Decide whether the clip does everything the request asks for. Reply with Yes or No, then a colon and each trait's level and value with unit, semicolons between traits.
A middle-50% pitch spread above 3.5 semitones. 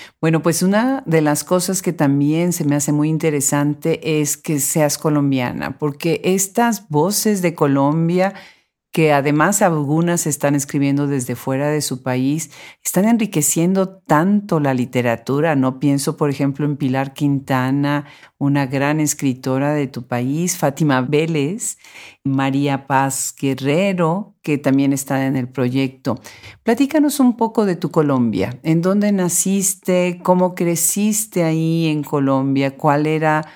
Yes: average, 4.0 semitones